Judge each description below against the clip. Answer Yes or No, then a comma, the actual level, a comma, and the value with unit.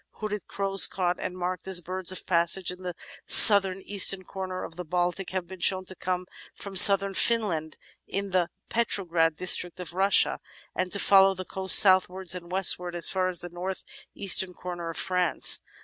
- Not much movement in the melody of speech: Yes, narrow, 1.5 semitones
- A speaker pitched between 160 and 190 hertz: Yes, medium, 185 Hz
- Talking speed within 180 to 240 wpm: Yes, average, 185 wpm